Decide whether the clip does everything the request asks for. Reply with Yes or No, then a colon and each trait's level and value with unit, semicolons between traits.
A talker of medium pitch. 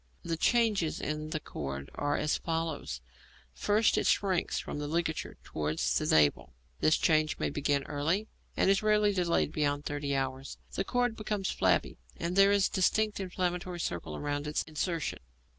Yes: medium, 160 Hz